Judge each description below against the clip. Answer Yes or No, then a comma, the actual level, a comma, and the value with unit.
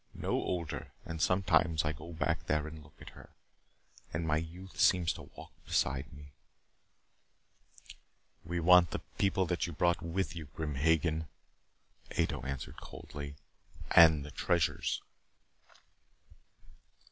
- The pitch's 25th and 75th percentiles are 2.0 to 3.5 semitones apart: Yes, narrow, 2.4 semitones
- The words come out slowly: Yes, slow, 130 wpm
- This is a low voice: Yes, very low, 80 Hz